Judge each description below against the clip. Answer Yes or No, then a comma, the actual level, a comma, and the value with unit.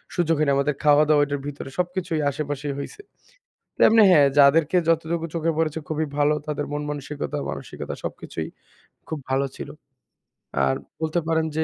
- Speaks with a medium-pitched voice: Yes, medium, 150 Hz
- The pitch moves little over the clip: Yes, narrow, 2.1 semitones